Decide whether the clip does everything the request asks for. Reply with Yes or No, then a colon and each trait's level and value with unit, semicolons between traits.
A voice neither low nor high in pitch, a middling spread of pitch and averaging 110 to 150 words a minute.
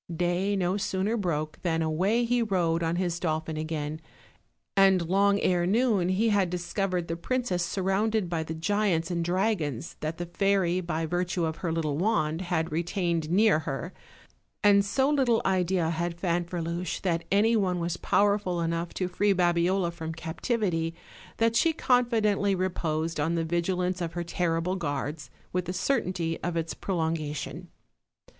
No: medium, 175 Hz; average, 3.0 semitones; average, 160 wpm